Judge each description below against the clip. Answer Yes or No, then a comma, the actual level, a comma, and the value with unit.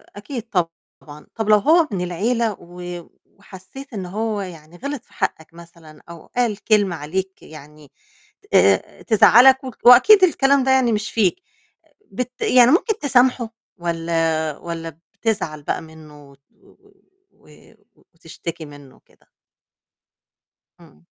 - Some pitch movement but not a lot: No, wide, 6.8 semitones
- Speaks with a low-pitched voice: No, high, 190 Hz